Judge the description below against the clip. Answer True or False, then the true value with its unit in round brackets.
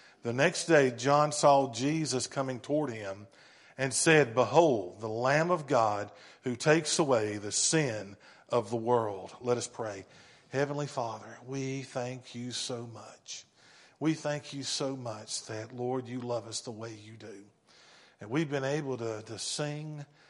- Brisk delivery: False (165 wpm)